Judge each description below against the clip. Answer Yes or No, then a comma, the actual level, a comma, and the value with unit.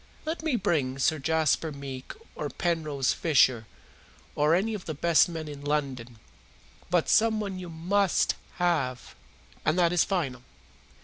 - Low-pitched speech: No, medium, 160 Hz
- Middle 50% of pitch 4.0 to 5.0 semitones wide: Yes, average, 4.3 semitones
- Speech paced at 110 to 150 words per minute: Yes, average, 140 wpm